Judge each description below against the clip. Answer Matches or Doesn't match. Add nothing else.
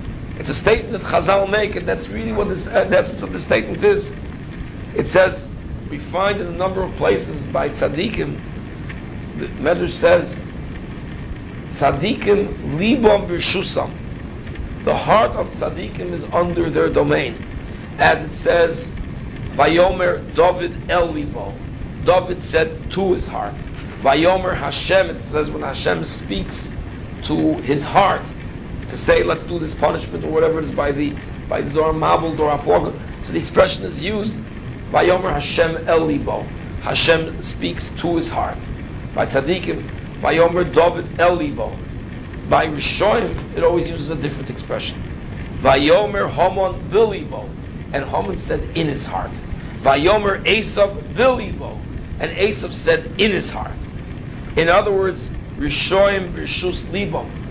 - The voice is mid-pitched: Matches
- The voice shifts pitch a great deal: Doesn't match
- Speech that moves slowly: Doesn't match